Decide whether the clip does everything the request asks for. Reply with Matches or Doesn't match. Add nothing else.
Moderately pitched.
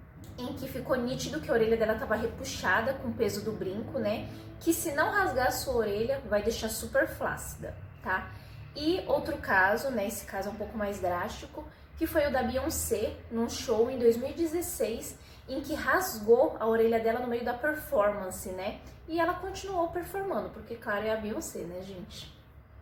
Doesn't match